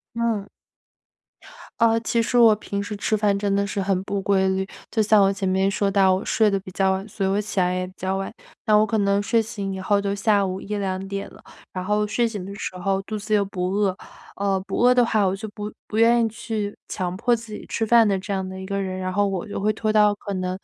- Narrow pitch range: Yes, narrow, 1.9 semitones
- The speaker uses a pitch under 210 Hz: Yes, high, 200 Hz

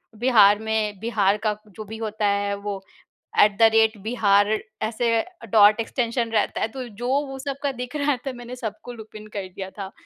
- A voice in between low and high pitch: No, high, 220 Hz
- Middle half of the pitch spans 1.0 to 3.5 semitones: Yes, average, 2.8 semitones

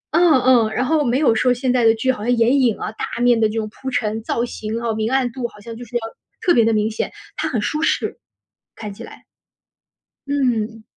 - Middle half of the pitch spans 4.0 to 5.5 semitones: No, narrow, 2.6 semitones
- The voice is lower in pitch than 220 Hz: No, high, 235 Hz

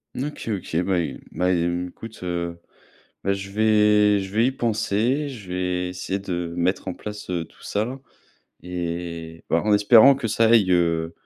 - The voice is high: No, very low, 95 Hz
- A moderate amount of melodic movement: Yes, average, 3.7 semitones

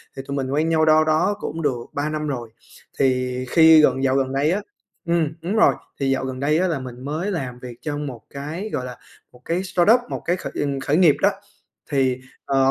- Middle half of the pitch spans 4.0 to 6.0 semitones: No, average, 3.6 semitones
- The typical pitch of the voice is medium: Yes, medium, 145 Hz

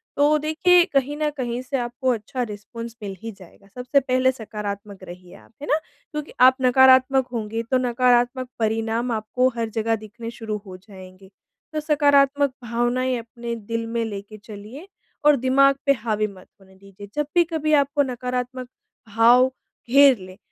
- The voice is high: Yes, high, 245 Hz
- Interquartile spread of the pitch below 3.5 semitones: No, average, 3.9 semitones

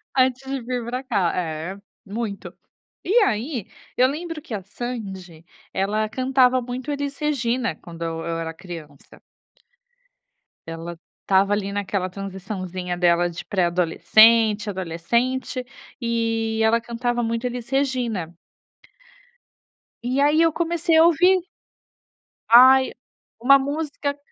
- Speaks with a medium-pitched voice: No, high, 230 Hz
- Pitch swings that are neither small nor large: No, wide, 5.8 semitones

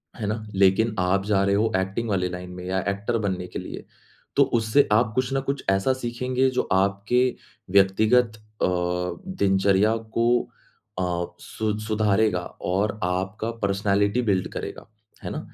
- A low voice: Yes, low, 100 Hz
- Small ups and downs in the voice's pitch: No, average, 3.1 semitones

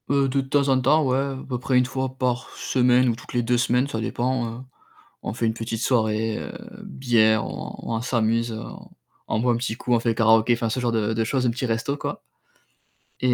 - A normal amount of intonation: No, narrow, 2.3 semitones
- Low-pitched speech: Yes, low, 120 Hz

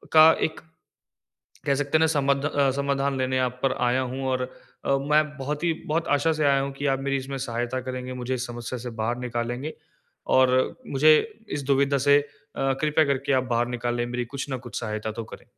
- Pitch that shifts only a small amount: Yes, narrow, 2.3 semitones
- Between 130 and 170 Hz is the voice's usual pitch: Yes, low, 135 Hz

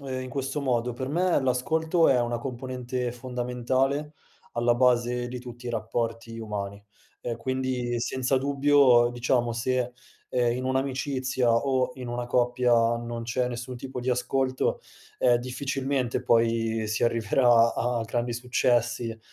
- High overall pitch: No, low, 125 Hz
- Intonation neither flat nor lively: No, narrow, 1.6 semitones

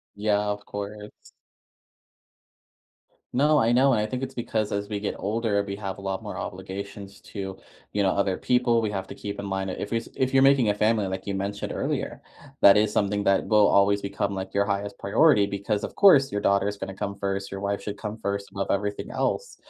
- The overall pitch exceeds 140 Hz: No, low, 100 Hz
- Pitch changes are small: Yes, narrow, 1.4 semitones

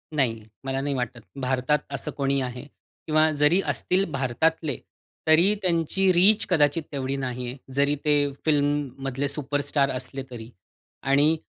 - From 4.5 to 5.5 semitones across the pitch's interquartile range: No, average, 2.9 semitones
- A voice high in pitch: No, medium, 140 Hz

